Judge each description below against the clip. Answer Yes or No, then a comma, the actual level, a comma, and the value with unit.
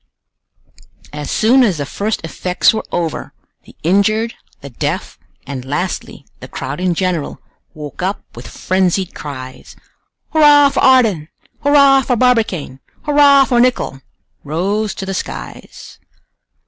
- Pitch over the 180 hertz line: Yes, high, 190 Hz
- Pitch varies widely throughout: Yes, wide, 8.6 semitones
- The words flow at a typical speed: No, slow, 130 wpm